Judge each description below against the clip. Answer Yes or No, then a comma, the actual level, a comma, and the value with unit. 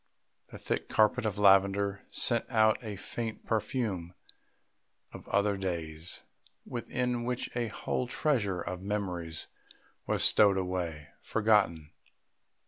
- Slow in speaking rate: Yes, slow, 115 wpm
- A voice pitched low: Yes, low, 100 Hz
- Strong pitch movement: No, average, 3.6 semitones